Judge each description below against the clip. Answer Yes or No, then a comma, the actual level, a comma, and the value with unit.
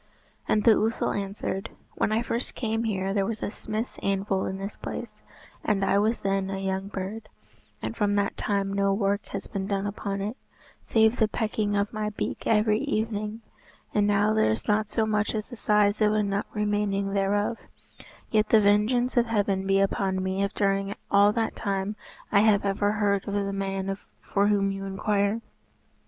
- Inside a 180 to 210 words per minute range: Yes, average, 190 wpm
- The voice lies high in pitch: Yes, high, 205 Hz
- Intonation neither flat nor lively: No, narrow, 1.6 semitones